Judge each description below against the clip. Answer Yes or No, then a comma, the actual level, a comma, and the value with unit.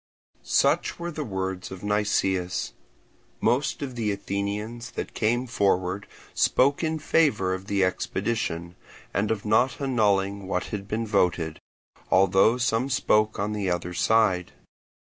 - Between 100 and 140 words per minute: Yes, slow, 135 wpm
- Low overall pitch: Yes, low, 105 Hz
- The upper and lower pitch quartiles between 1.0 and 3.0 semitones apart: No, average, 3.5 semitones